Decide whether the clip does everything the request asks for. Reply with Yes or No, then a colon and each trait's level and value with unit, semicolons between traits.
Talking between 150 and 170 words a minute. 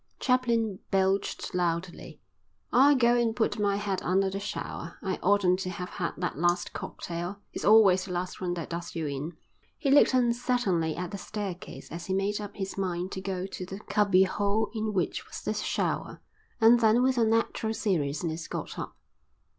No: average, 180 wpm